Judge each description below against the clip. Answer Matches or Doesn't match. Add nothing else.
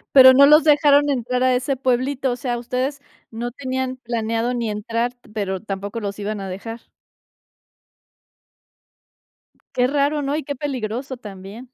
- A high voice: Matches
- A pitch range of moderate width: Matches